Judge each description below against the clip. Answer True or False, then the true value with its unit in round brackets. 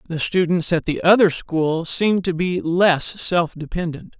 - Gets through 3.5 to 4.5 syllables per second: True (4.3 syllables/s)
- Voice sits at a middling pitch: True (175 Hz)